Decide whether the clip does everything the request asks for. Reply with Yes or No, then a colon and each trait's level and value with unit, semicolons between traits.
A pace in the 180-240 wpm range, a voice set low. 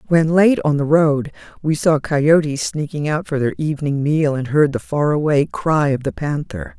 No: fast, 205 wpm; medium, 150 Hz